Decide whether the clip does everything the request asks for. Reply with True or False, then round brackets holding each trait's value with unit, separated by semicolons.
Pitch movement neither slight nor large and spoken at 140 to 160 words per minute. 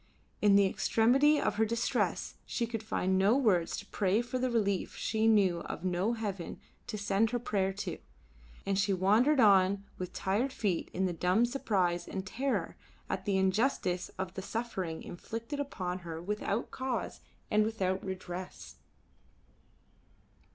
True (3.5 semitones; 150 wpm)